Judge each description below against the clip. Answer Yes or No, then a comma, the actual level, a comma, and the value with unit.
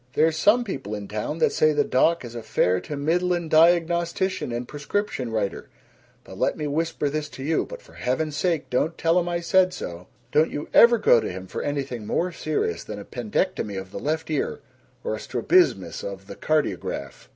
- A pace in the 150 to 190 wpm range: No, average, 200 wpm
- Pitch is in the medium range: Yes, medium, 155 Hz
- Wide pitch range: Yes, wide, 5.9 semitones